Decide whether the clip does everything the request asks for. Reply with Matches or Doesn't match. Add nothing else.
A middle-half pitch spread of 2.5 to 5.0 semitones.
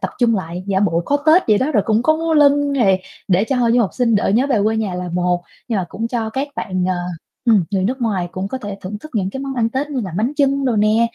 Doesn't match